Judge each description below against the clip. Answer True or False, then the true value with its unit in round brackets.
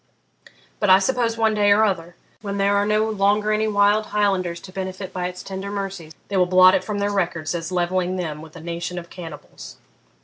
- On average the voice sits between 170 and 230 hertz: True (190 Hz)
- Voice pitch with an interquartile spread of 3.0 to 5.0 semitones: False (2.5 semitones)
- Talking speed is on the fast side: True (210 wpm)